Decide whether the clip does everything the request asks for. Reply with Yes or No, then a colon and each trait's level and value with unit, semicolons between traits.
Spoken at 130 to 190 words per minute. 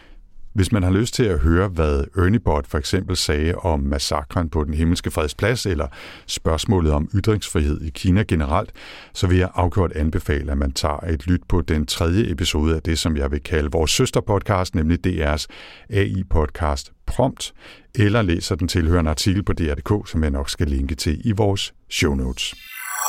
Yes: average, 180 wpm